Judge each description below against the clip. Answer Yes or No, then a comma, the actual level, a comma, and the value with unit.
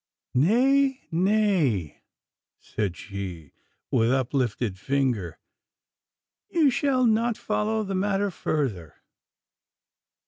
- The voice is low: No, medium, 155 Hz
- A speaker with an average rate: No, slow, 80 wpm